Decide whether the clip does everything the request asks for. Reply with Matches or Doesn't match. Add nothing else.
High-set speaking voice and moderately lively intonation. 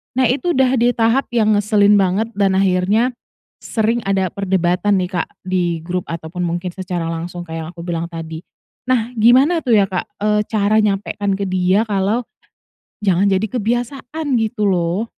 Matches